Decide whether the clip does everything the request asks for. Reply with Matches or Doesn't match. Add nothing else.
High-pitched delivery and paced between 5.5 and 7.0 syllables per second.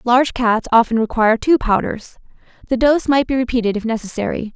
Matches